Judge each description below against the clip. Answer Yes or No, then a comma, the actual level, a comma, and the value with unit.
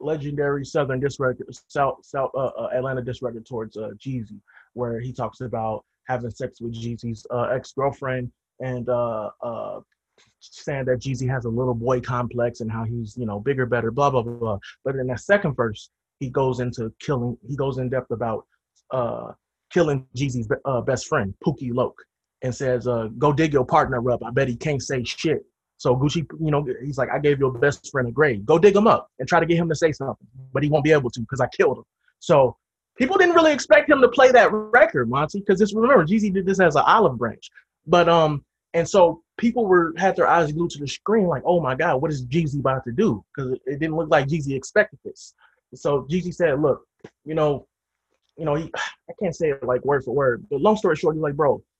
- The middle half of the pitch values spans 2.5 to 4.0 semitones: No, average, 4.7 semitones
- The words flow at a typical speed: No, fast, 220 wpm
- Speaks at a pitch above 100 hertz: Yes, low, 135 Hz